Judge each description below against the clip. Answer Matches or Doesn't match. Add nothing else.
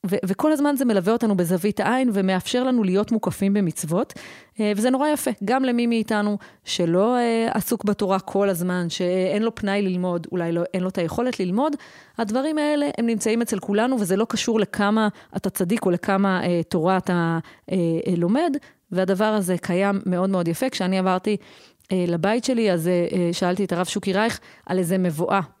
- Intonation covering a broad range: Doesn't match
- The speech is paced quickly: Matches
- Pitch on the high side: Matches